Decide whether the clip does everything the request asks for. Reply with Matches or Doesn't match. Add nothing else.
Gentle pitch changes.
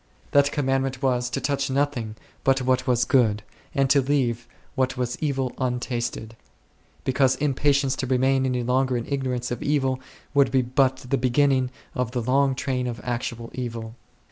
Matches